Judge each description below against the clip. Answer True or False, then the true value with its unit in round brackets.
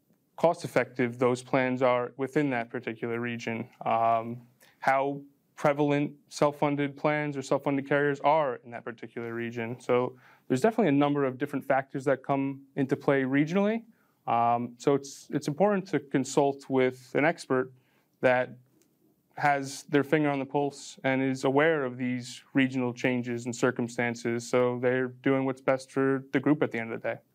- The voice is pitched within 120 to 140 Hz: True (135 Hz)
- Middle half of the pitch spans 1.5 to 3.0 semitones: True (2.5 semitones)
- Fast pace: False (170 wpm)